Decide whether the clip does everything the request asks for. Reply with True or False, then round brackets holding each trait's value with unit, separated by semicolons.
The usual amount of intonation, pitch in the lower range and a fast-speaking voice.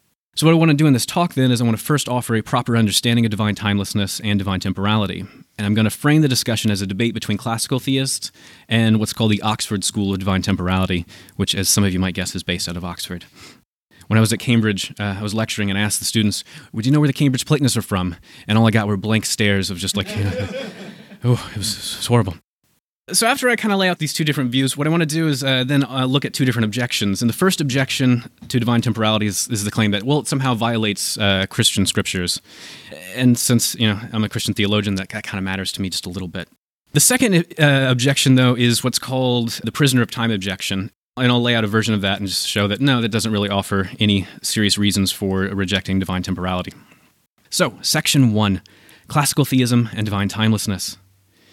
True (4.5 semitones; 110 Hz; 240 wpm)